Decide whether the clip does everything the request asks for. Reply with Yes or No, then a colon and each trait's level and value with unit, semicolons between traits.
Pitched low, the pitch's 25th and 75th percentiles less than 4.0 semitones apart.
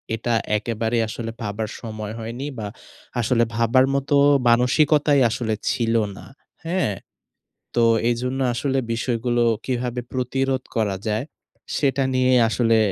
Yes: low, 120 Hz; narrow, 2.4 semitones